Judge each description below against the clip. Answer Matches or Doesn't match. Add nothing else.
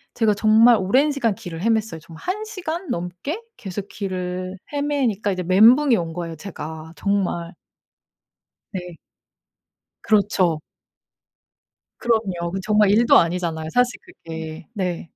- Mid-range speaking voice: Doesn't match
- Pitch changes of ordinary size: Matches